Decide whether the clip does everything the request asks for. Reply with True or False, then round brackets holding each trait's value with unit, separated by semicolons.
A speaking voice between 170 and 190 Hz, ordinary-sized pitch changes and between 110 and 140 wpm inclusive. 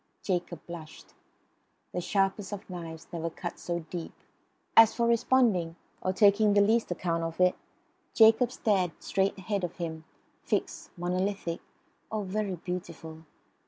True (185 Hz; 3.3 semitones; 135 wpm)